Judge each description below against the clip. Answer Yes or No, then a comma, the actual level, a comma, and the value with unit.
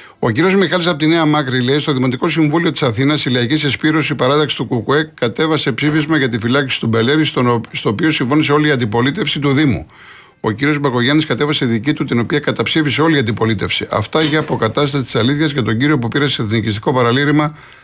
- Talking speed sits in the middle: No, fast, 200 wpm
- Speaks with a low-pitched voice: No, medium, 145 Hz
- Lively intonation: No, average, 3.6 semitones